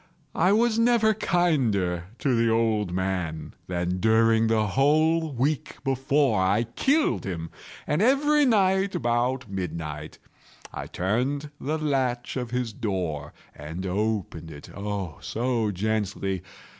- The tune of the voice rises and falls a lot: Yes, wide, 7.8 semitones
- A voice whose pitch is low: Yes, low, 115 Hz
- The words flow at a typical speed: No, slow, 120 wpm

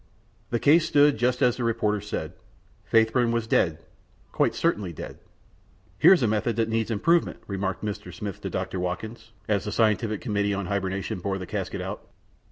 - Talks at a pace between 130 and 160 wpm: No, average, 175 wpm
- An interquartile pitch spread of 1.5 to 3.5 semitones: Yes, average, 2.9 semitones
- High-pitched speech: No, low, 110 Hz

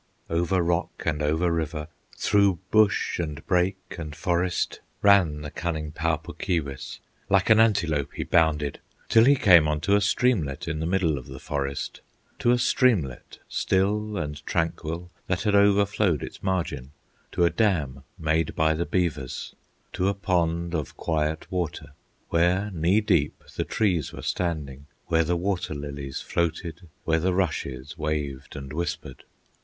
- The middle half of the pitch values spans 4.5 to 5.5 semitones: No, average, 3.8 semitones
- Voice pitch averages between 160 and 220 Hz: No, very low, 85 Hz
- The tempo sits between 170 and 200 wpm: No, average, 155 wpm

